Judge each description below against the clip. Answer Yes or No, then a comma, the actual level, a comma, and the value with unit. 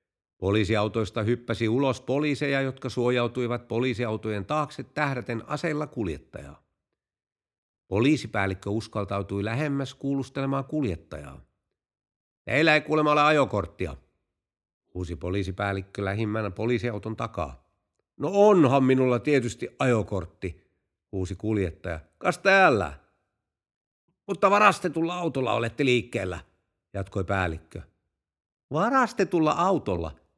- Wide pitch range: Yes, wide, 6.6 semitones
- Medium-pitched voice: No, low, 115 Hz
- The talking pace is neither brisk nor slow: No, slow, 85 wpm